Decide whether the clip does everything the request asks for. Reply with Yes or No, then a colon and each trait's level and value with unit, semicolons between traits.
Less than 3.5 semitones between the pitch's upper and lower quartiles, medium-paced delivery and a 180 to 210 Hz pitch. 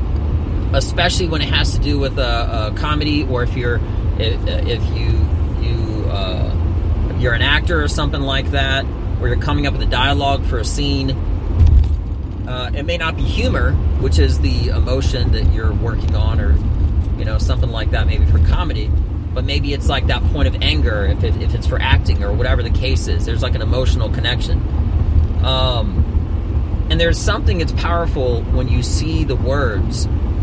No: average, 2.8 semitones; average, 185 wpm; very low, 85 Hz